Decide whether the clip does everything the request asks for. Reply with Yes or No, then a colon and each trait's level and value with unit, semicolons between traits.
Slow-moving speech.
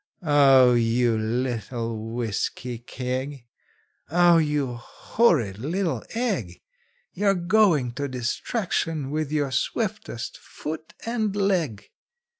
Yes: slow, 95 wpm